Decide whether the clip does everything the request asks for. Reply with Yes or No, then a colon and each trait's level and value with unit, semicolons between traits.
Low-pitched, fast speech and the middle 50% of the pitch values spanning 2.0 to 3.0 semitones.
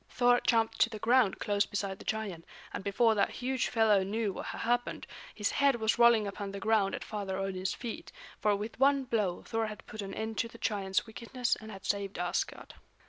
No: high, 215 Hz; fast, 210 wpm; average, 2.7 semitones